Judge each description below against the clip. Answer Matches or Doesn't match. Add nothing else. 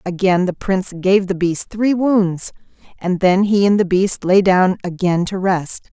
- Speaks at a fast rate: Doesn't match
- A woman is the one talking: Matches